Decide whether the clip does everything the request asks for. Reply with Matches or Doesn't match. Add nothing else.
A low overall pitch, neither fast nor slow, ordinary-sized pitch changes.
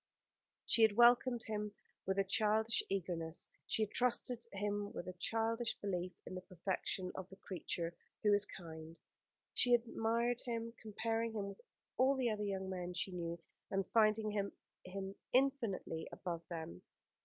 Doesn't match